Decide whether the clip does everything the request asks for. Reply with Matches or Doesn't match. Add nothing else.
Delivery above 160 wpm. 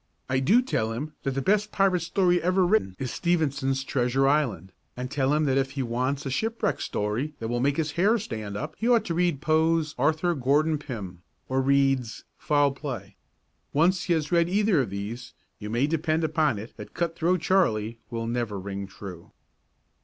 Matches